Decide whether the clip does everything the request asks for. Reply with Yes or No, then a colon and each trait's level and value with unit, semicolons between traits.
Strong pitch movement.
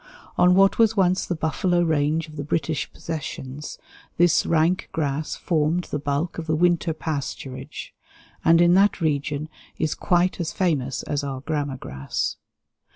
No: average, 3.3 semitones